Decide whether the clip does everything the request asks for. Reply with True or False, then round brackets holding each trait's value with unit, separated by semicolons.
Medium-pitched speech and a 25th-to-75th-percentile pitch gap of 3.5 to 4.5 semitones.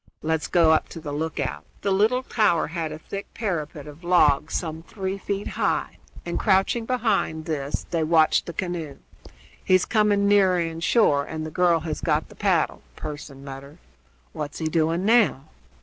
True (165 Hz; 3.9 semitones)